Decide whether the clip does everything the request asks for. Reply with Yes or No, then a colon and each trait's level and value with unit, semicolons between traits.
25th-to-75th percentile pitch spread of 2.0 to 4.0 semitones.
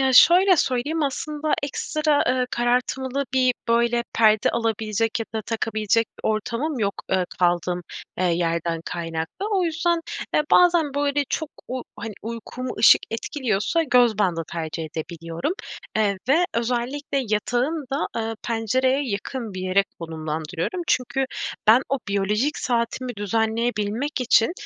No: average, 5.1 semitones